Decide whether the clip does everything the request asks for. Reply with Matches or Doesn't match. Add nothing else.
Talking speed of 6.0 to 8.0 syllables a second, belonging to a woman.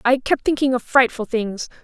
Doesn't match